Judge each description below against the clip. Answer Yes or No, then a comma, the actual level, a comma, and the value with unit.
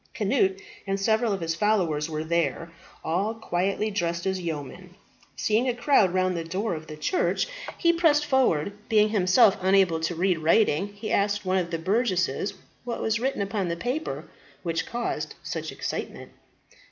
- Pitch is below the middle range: No, high, 195 Hz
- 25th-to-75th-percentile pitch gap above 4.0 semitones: Yes, average, 4.7 semitones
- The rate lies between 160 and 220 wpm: Yes, average, 165 wpm